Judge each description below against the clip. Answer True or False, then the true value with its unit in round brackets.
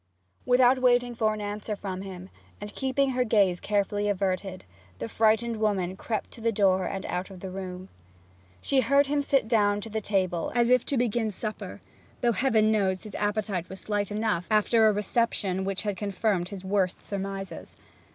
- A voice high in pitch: True (205 Hz)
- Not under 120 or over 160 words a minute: False (180 wpm)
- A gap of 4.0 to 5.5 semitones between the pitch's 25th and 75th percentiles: False (3.0 semitones)